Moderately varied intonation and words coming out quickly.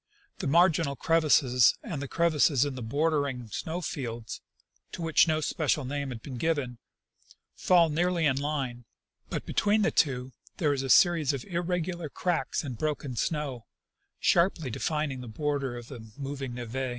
No: average, 4.2 semitones; average, 165 wpm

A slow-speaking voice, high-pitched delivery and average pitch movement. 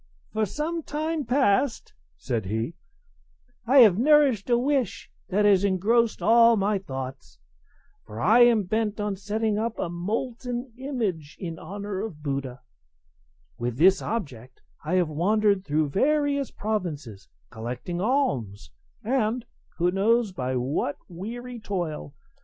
No: slow, 130 wpm; high, 205 Hz; wide, 7.3 semitones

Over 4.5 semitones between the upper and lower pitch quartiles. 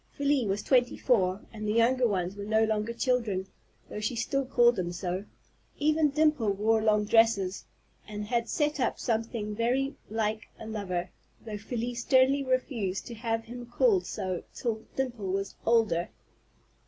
No: average, 3.3 semitones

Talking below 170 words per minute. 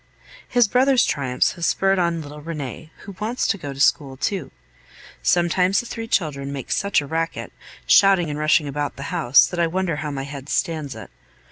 No: average, 195 wpm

